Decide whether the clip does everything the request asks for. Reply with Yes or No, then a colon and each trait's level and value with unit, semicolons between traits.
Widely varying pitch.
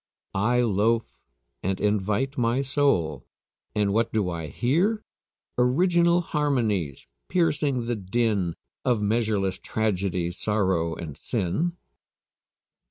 Yes: wide, 5.7 semitones